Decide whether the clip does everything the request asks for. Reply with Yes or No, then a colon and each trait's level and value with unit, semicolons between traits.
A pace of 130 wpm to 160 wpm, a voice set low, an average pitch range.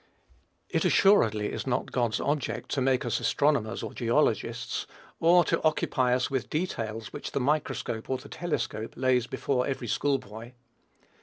Yes: average, 155 wpm; low, 125 Hz; average, 3.9 semitones